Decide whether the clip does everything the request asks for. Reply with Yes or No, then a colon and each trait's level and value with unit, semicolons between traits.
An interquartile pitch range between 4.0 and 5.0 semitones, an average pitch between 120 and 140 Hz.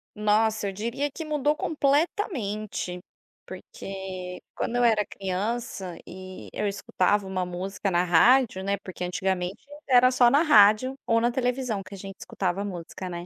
No: average, 4.6 semitones; high, 205 Hz